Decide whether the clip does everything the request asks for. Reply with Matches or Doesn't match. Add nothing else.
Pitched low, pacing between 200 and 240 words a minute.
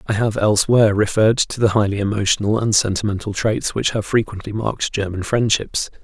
Doesn't match